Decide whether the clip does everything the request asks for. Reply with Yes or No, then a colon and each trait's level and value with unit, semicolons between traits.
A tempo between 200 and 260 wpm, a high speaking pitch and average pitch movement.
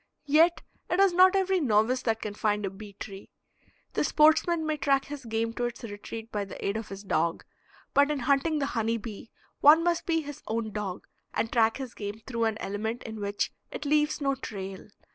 No: fast, 205 wpm; high, 230 Hz; wide, 5.9 semitones